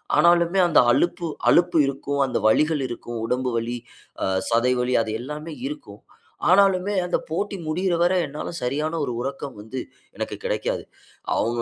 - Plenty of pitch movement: Yes, wide, 5.8 semitones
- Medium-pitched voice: Yes, medium, 145 Hz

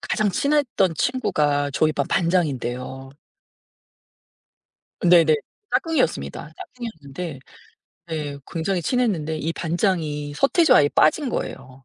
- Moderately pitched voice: Yes, medium, 160 Hz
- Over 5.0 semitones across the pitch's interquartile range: Yes, wide, 5.5 semitones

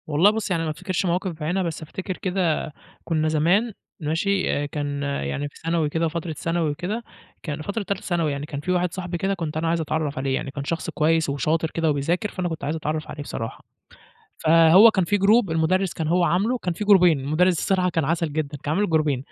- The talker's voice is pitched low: No, medium, 165 Hz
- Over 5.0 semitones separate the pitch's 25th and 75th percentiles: No, average, 3.2 semitones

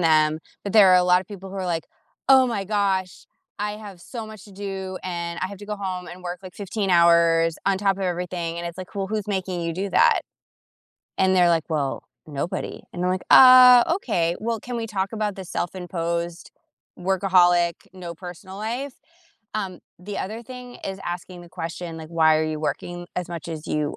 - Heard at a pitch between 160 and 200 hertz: Yes, medium, 185 Hz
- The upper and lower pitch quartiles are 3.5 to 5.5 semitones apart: No, average, 2.9 semitones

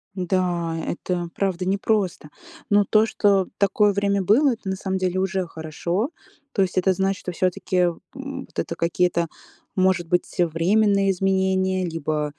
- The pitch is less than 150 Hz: No, high, 190 Hz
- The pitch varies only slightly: Yes, narrow, 2.1 semitones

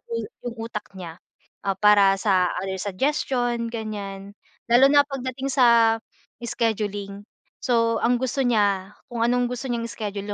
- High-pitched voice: Yes, high, 230 Hz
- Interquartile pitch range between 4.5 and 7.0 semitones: No, average, 3.4 semitones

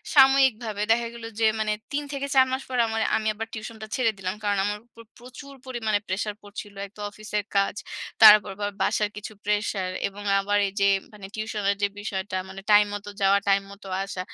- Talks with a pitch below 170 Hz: No, high, 210 Hz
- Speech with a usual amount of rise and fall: No, narrow, 2.1 semitones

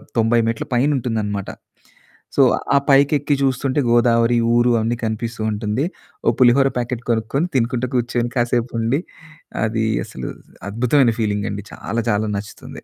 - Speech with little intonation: Yes, narrow, 2.2 semitones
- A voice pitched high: No, low, 120 Hz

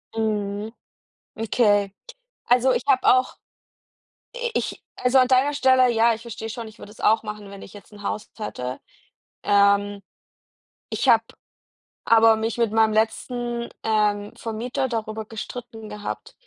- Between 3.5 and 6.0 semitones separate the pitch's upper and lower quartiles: No, narrow, 2.5 semitones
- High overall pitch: Yes, high, 225 Hz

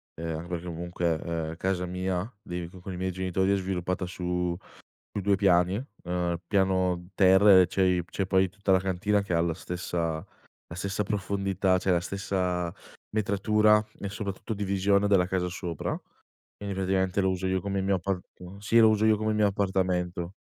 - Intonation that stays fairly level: Yes, narrow, 1.9 semitones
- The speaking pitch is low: Yes, very low, 95 Hz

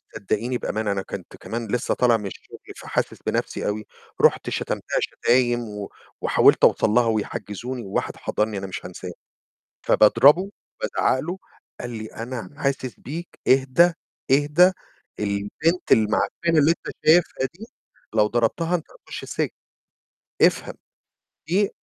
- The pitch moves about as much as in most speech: No, wide, 6.4 semitones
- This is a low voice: Yes, low, 120 Hz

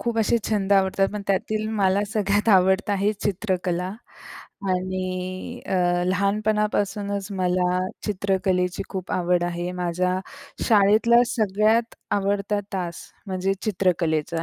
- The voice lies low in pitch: No, high, 195 Hz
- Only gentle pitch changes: Yes, narrow, 2.3 semitones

